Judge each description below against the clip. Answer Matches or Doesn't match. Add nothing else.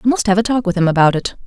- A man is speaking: Doesn't match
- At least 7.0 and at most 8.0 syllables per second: Matches